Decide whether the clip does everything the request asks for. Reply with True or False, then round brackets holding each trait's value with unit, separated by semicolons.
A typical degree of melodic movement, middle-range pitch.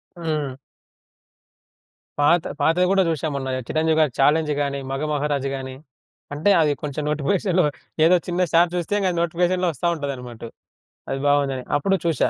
True (3.7 semitones; 150 Hz)